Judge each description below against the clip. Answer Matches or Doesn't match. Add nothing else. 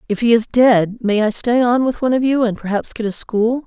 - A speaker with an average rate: Doesn't match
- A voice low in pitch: Doesn't match